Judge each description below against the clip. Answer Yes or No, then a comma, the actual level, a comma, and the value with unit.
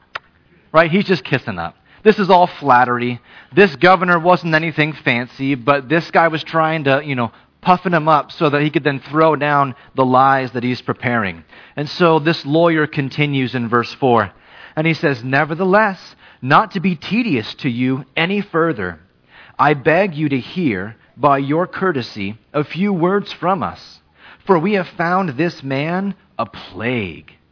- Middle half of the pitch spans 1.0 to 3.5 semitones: No, average, 5.2 semitones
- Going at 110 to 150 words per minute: No, average, 170 wpm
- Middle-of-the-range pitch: Yes, medium, 150 Hz